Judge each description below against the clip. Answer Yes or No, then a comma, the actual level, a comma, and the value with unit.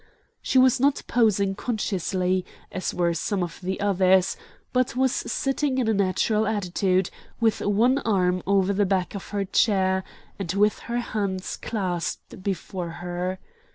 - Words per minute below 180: Yes, average, 150 wpm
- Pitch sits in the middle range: No, high, 195 Hz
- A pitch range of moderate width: Yes, average, 3.0 semitones